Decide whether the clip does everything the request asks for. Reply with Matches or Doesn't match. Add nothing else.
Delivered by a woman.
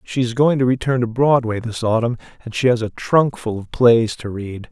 Doesn't match